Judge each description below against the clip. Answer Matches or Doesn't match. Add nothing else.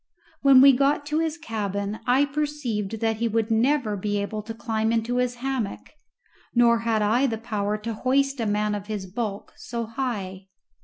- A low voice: Doesn't match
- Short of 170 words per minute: Doesn't match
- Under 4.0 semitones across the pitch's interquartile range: Matches